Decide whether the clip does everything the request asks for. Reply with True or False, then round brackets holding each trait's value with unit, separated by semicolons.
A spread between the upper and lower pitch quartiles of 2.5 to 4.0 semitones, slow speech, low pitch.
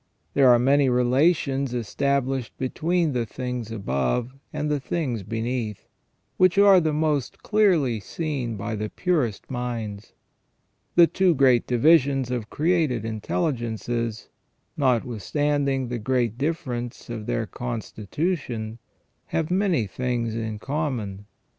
False (4.5 semitones; 115 wpm; 125 Hz)